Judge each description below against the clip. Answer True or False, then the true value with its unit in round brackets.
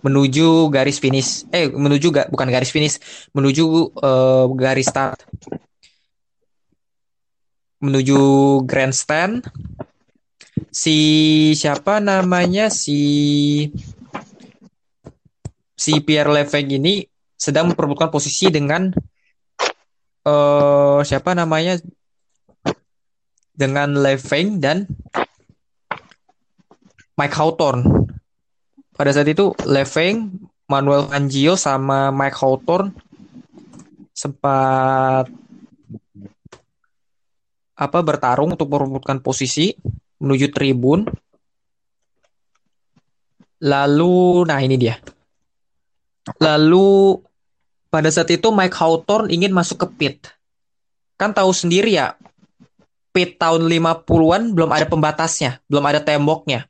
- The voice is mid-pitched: True (150 Hz)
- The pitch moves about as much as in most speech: True (3.7 semitones)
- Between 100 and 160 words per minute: False (85 wpm)